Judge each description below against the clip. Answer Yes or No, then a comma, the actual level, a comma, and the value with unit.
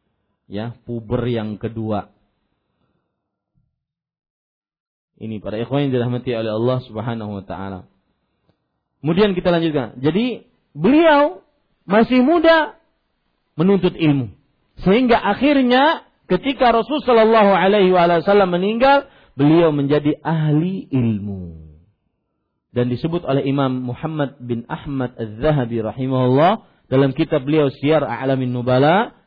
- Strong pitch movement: Yes, wide, 8.4 semitones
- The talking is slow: No, average, 105 wpm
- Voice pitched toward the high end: No, medium, 140 Hz